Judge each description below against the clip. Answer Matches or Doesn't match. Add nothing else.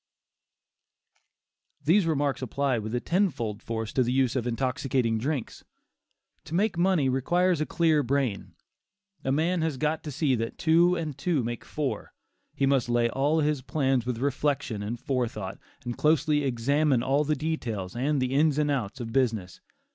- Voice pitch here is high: Doesn't match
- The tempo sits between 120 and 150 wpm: Doesn't match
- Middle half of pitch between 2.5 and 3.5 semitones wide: Doesn't match